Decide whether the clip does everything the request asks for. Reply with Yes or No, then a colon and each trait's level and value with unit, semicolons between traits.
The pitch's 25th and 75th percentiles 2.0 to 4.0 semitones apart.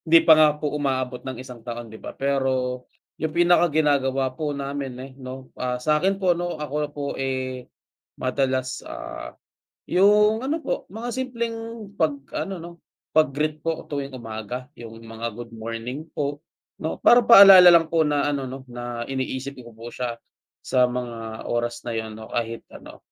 No: average, 4.4 semitones